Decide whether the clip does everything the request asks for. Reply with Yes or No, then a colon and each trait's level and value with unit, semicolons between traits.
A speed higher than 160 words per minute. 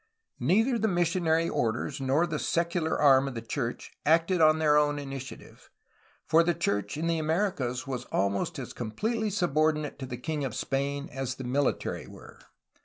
Yes: average, 170 wpm